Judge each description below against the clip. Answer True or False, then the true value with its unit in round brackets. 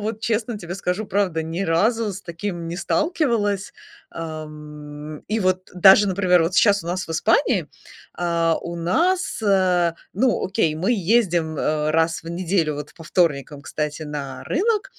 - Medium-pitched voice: True (180 Hz)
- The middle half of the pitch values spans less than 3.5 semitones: False (4.3 semitones)